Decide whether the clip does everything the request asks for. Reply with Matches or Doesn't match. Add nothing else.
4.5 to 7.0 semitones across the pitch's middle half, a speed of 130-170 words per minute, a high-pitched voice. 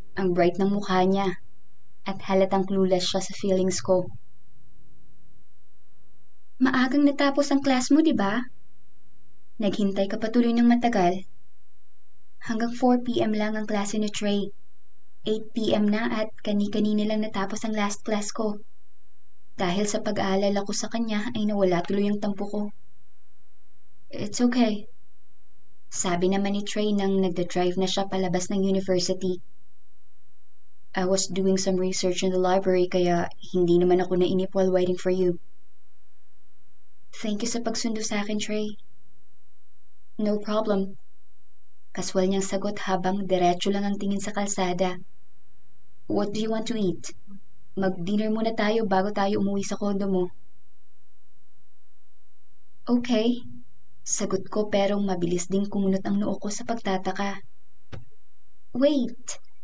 Doesn't match